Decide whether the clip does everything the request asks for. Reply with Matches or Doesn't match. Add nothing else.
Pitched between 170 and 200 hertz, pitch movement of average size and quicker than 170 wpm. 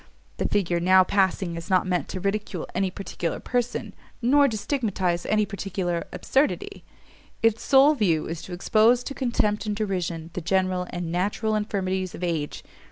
Doesn't match